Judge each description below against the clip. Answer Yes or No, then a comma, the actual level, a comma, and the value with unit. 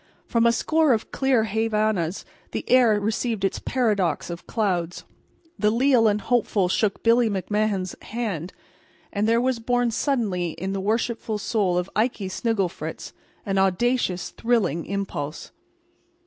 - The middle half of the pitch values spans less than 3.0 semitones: No, average, 3.6 semitones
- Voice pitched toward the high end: Yes, high, 215 Hz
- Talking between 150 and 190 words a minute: No, average, 140 wpm